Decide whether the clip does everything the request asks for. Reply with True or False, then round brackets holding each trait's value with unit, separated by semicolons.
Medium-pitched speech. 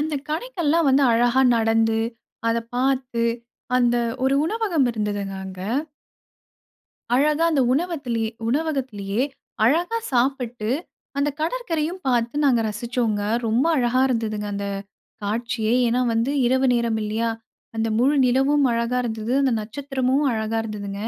False (245 Hz)